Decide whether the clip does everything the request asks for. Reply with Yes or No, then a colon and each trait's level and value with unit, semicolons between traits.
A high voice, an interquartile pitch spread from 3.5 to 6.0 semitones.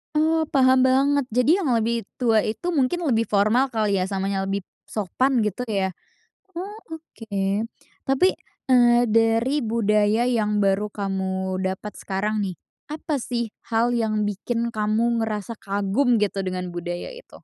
Yes: high, 225 Hz; average, 3.9 semitones